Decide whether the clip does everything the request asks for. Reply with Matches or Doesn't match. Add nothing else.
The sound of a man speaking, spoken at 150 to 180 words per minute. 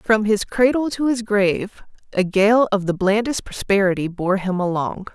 Doesn't match